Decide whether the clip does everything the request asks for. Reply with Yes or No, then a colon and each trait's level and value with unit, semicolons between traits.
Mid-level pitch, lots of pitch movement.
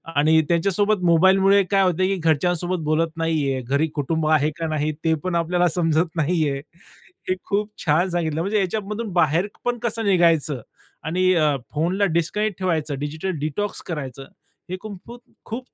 No: medium, 170 Hz; average, 3.6 semitones